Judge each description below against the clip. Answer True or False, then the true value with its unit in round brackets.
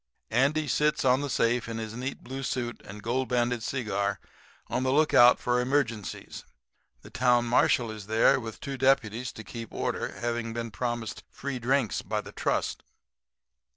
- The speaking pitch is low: True (120 Hz)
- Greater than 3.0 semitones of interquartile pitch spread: False (2.6 semitones)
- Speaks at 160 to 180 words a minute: True (165 wpm)